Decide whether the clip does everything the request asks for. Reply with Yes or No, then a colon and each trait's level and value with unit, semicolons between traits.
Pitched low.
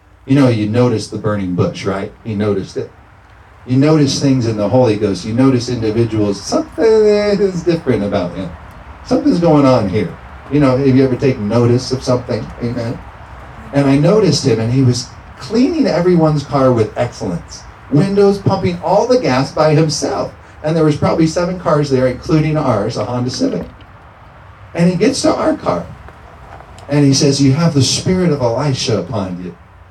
Yes: low, 130 Hz